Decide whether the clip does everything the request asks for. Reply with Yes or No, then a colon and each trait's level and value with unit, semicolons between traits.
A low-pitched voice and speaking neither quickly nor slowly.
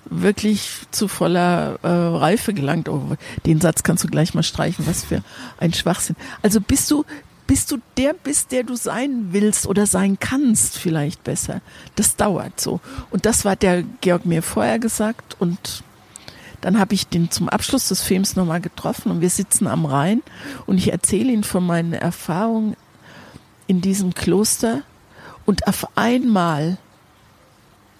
No: high, 195 Hz; average, 160 wpm